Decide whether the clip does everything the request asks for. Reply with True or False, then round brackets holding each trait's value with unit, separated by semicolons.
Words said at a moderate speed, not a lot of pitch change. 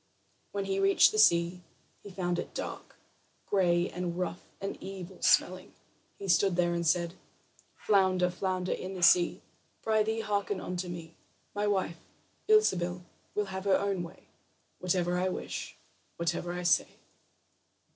True (145 wpm; 2.0 semitones)